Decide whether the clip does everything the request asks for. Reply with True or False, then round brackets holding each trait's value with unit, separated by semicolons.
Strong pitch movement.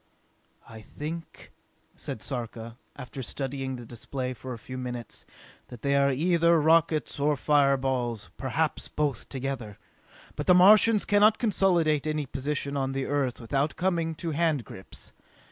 False (4.1 semitones)